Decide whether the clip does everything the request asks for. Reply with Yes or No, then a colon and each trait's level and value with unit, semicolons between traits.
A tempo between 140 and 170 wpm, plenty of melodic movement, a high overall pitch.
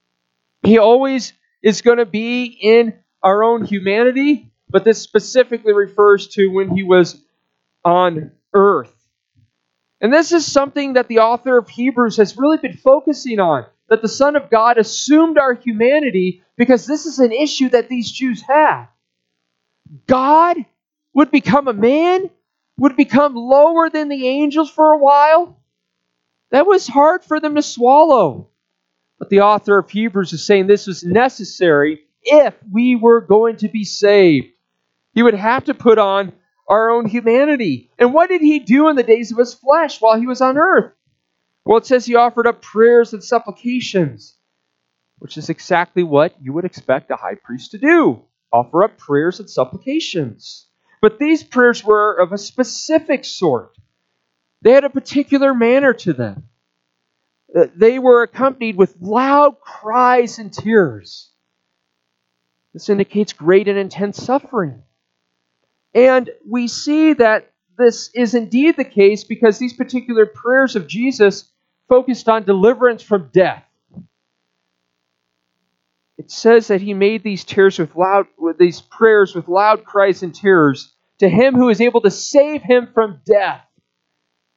Yes: average, 155 wpm; wide, 6.7 semitones; high, 220 Hz